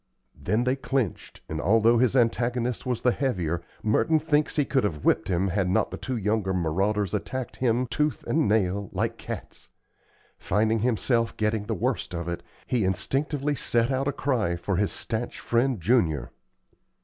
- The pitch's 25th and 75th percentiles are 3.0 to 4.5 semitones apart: No, average, 5.0 semitones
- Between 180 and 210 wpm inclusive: No, average, 170 wpm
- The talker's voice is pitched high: No, low, 115 Hz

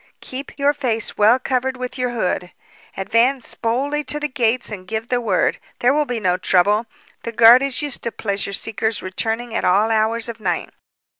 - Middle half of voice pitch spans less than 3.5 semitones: Yes, average, 3.1 semitones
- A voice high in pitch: Yes, high, 230 Hz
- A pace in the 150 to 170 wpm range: No, average, 190 wpm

